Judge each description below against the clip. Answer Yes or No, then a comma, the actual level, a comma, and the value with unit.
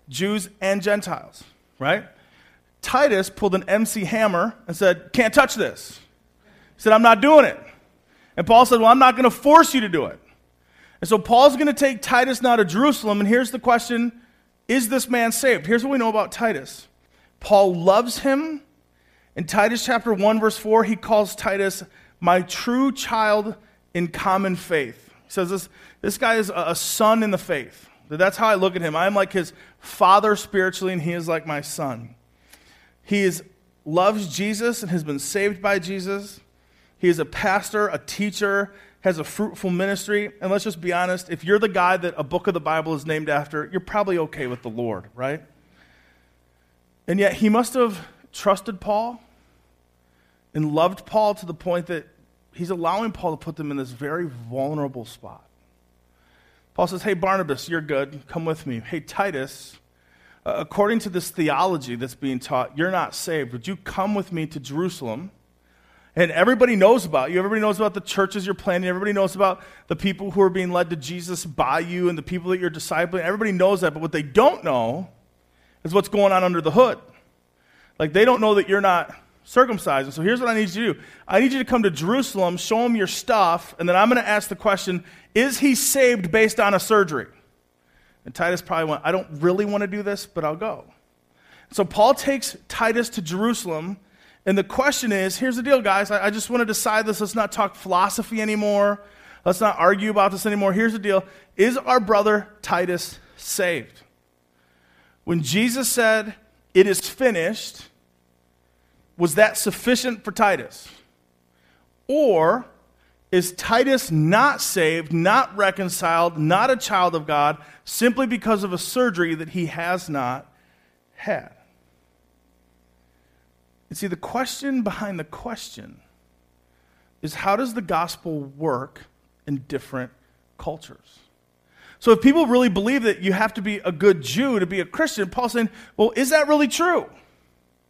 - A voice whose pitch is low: No, medium, 185 Hz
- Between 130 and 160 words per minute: No, average, 180 wpm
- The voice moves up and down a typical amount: No, wide, 6.6 semitones